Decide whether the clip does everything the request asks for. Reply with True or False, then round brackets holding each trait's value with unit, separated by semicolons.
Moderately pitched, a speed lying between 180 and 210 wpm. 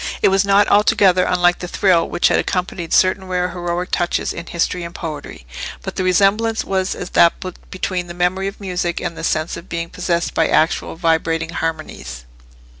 True (180 Hz; 185 wpm)